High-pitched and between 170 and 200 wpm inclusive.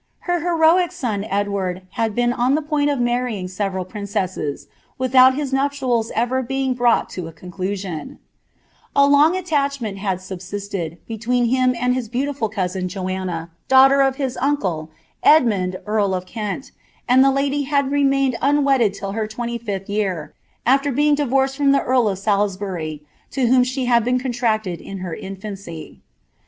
No: high, 235 Hz; average, 150 wpm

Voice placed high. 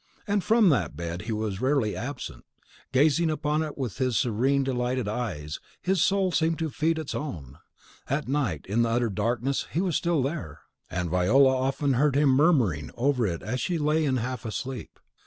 No: low, 130 Hz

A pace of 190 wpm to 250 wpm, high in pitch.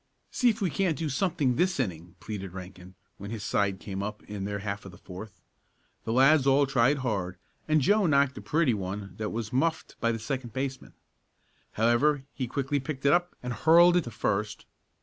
No: average, 200 wpm; low, 125 Hz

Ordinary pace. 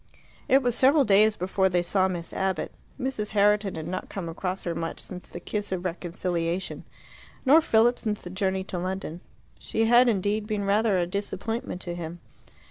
Yes: average, 180 wpm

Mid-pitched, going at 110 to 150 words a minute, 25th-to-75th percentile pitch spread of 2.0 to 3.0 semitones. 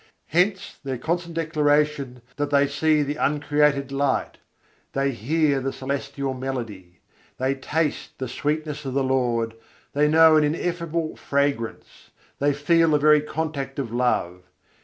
Yes: medium, 145 Hz; average, 140 wpm; narrow, 2.5 semitones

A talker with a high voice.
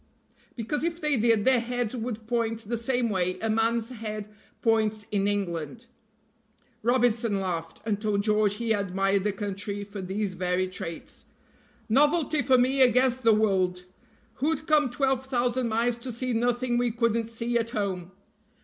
Yes: high, 225 Hz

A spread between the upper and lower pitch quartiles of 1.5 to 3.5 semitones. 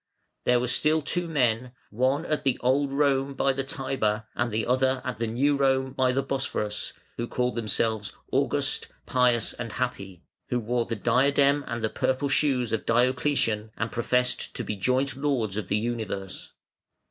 Yes: average, 3.1 semitones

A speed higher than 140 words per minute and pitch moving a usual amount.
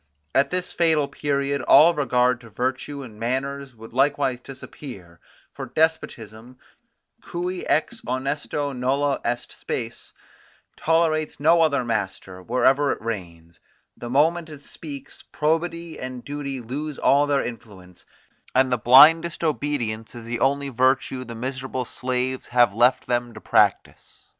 No: slow, 135 wpm; average, 3.3 semitones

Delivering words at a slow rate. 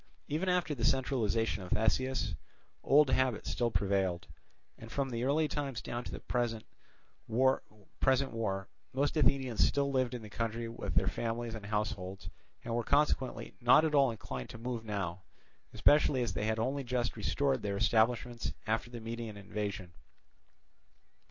No: average, 155 wpm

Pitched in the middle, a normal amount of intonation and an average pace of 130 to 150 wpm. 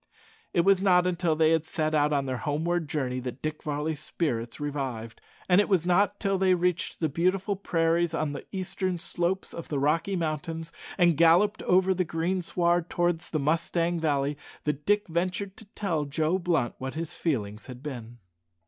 No: medium, 165 Hz; average, 3.4 semitones; average, 180 wpm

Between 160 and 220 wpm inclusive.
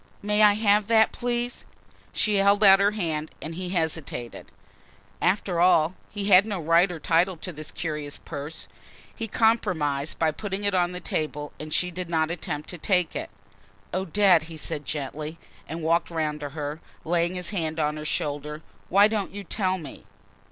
Yes: average, 180 wpm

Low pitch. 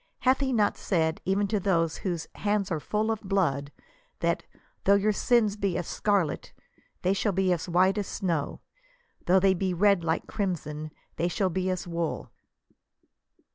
No: high, 190 Hz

